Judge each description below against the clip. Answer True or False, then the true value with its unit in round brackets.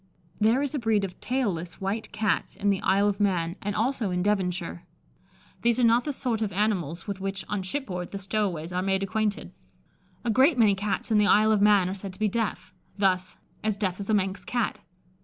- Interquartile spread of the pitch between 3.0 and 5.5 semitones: False (2.6 semitones)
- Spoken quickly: True (220 wpm)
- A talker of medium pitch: False (205 Hz)